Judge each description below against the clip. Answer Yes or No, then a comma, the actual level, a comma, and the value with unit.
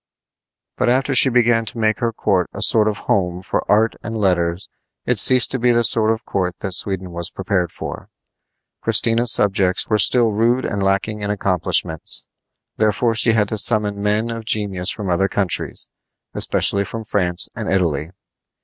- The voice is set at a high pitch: No, low, 105 Hz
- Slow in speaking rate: No, average, 175 wpm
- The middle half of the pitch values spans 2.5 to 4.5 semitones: Yes, average, 3.2 semitones